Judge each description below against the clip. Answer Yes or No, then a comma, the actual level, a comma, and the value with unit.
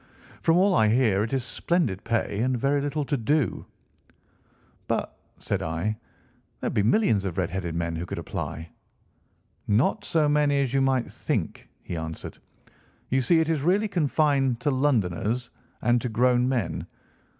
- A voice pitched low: Yes, low, 125 Hz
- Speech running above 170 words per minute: No, average, 165 wpm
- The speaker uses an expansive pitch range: Yes, wide, 6.0 semitones